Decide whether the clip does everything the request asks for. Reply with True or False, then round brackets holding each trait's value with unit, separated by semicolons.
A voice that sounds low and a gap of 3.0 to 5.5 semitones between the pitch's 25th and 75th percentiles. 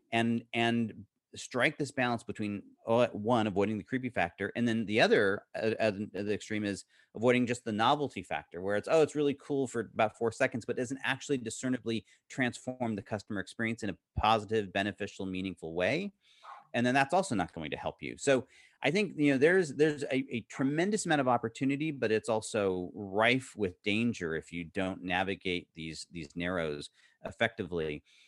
True (115 Hz; 4.4 semitones)